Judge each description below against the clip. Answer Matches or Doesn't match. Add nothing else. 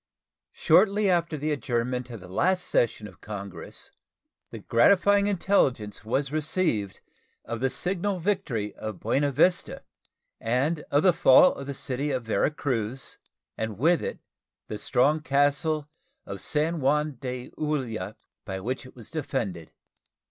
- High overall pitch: Doesn't match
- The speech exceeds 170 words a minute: Doesn't match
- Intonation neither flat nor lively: Doesn't match